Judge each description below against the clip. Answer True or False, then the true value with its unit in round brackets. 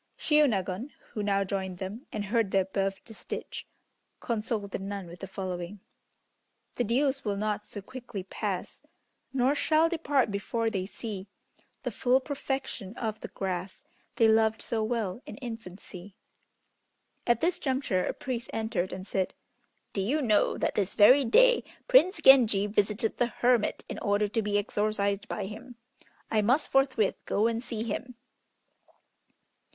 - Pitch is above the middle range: True (215 Hz)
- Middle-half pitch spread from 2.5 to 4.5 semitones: True (3.9 semitones)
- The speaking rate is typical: True (150 wpm)